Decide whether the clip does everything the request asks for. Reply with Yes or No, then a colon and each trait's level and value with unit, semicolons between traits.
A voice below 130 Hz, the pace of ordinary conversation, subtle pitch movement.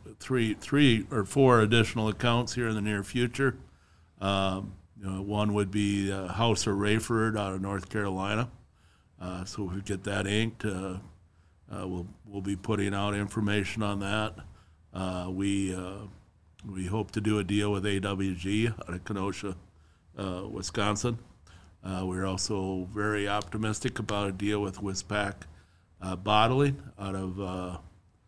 Yes: low, 100 Hz; average, 155 wpm; narrow, 2.3 semitones